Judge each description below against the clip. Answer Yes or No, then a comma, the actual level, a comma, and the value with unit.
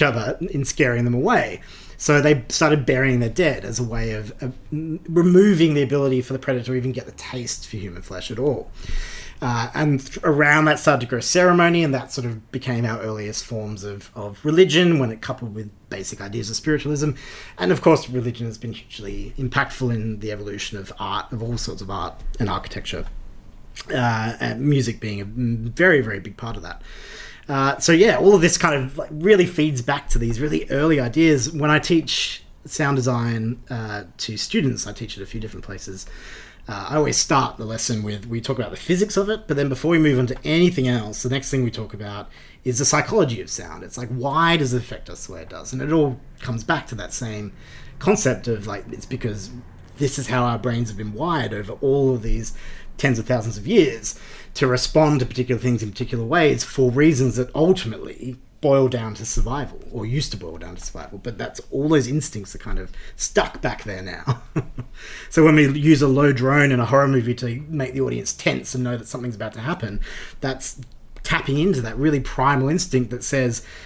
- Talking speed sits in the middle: No, fast, 215 wpm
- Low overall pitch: Yes, low, 125 Hz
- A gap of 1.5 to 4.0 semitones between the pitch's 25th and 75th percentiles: No, average, 4.4 semitones